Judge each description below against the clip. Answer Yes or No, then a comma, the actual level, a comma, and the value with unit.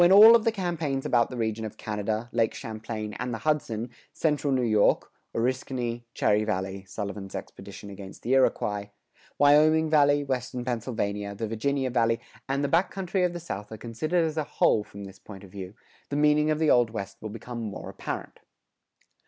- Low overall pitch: Yes, low, 120 Hz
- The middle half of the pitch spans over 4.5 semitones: Yes, wide, 5.6 semitones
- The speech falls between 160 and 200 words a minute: Yes, average, 185 wpm